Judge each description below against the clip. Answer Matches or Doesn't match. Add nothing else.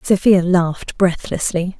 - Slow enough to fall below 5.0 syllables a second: Matches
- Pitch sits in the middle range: Matches